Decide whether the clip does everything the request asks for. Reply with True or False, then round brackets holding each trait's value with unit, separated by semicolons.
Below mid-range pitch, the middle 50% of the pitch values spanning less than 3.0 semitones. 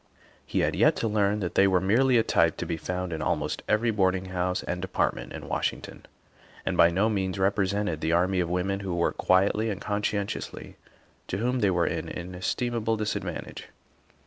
True (95 Hz; 2.6 semitones)